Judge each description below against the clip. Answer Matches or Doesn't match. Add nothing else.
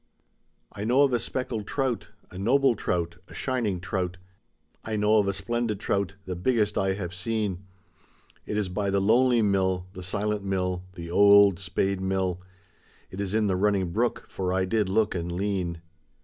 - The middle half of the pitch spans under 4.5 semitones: Matches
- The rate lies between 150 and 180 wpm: Matches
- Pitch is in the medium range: Doesn't match